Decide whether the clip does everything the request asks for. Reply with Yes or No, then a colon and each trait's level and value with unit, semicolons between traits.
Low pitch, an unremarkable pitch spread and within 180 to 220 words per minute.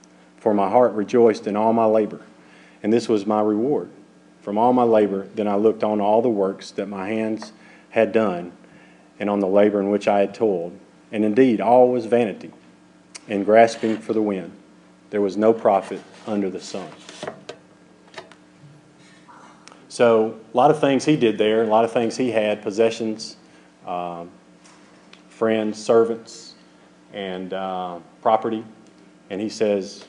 No: low, 105 Hz; average, 3.5 semitones; average, 160 wpm